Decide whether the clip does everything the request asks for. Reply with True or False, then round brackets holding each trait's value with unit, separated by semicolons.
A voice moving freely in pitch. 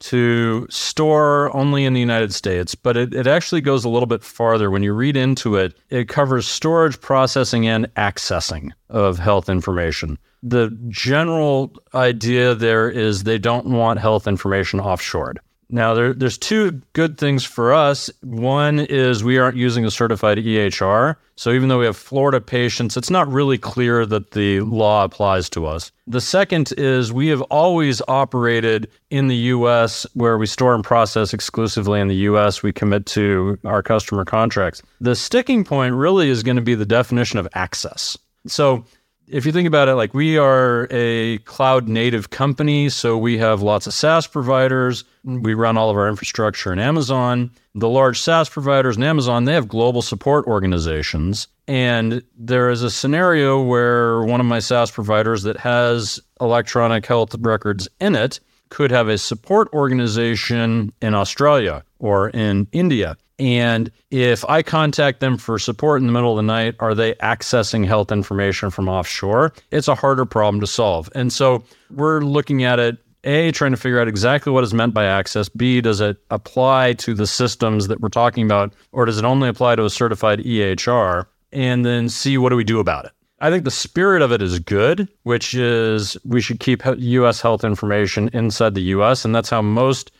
False (3.3 semitones)